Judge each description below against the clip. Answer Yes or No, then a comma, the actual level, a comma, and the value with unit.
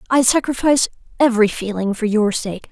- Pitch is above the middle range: Yes, high, 230 Hz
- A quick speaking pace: No, average, 155 wpm